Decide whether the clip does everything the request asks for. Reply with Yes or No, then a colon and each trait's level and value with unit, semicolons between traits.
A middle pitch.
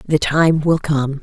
Yes: medium, 150 Hz